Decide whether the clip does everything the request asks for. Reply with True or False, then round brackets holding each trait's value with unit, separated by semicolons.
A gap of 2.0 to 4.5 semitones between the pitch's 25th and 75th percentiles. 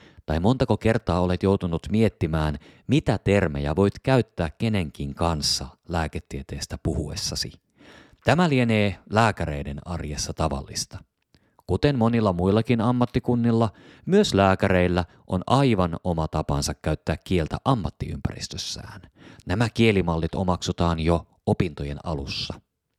False (5.6 semitones)